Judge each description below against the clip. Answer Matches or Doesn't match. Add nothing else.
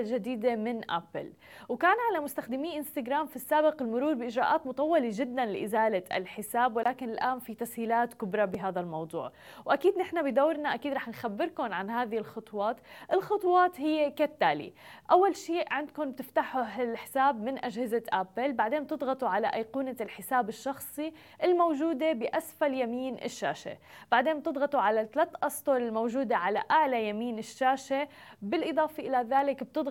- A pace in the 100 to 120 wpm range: Doesn't match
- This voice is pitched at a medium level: Doesn't match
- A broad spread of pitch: Doesn't match